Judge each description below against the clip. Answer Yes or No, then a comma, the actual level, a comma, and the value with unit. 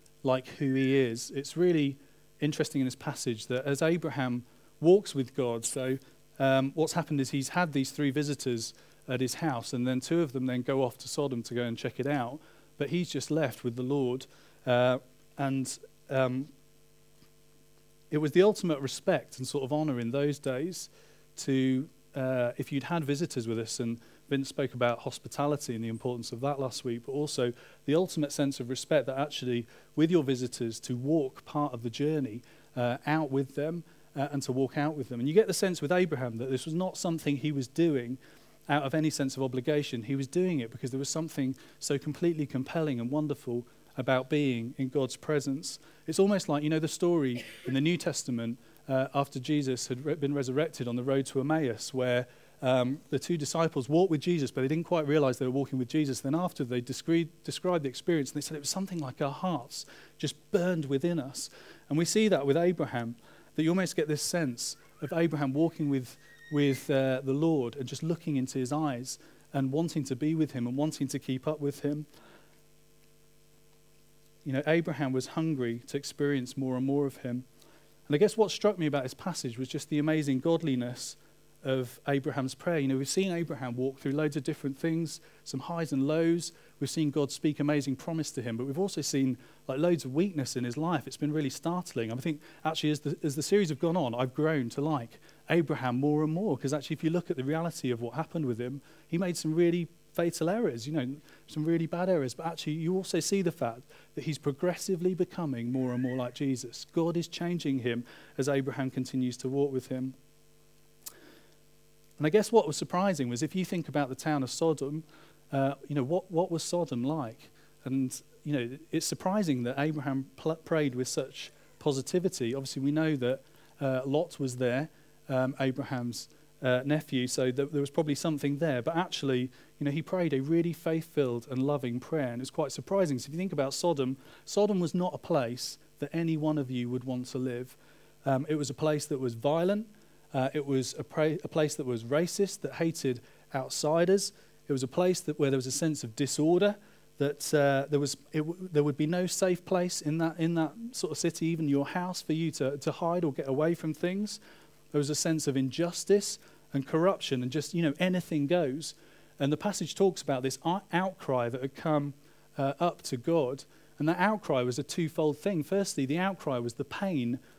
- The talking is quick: Yes, fast, 210 wpm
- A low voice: No, medium, 150 Hz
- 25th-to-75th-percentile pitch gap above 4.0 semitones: No, average, 3.3 semitones